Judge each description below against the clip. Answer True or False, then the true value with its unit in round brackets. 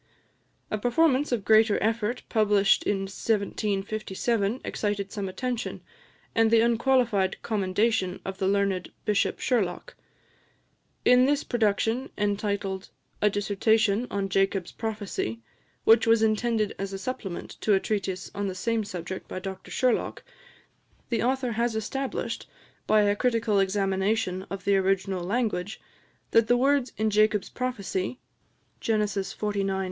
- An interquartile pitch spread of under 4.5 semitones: True (2.8 semitones)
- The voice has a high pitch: True (210 Hz)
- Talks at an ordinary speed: False (130 wpm)